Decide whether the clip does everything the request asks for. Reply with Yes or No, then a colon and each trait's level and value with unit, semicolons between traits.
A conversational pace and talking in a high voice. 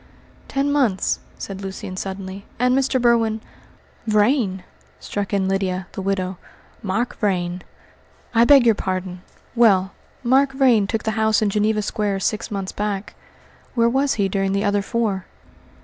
Yes: average, 150 wpm; high, 205 Hz